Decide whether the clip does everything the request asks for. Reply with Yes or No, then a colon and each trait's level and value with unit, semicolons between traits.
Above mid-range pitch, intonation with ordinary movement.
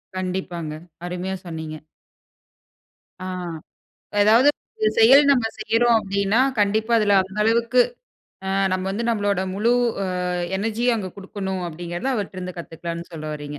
Yes: high, 195 Hz; average, 3.9 semitones